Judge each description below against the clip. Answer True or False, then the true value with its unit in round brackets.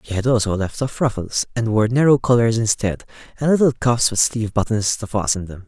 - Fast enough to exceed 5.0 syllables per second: True (5.7 syllables/s)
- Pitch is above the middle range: False (115 Hz)